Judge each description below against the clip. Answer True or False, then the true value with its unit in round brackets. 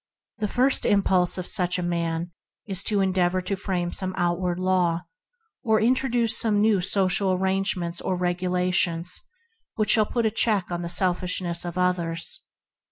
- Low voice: False (185 Hz)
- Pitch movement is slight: True (2.3 semitones)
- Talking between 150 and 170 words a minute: True (165 wpm)